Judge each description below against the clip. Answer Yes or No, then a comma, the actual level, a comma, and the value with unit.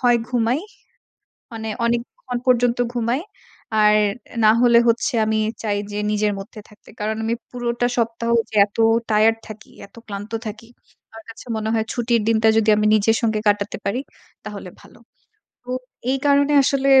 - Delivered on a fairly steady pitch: Yes, narrow, 2.1 semitones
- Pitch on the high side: Yes, high, 225 Hz